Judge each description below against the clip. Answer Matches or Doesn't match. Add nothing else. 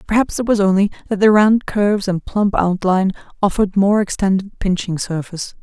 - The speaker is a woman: Matches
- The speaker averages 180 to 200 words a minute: Doesn't match